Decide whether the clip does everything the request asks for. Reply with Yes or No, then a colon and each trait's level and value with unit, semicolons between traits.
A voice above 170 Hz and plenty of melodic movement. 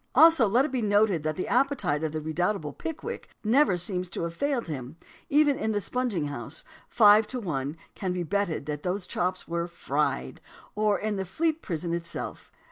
Yes: high, 190 Hz; wide, 5.8 semitones